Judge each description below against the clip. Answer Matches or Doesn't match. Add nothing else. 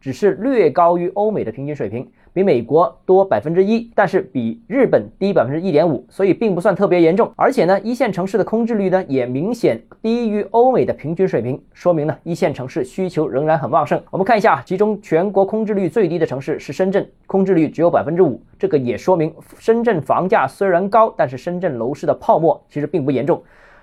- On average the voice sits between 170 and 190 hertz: Matches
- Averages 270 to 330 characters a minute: Doesn't match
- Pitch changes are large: Doesn't match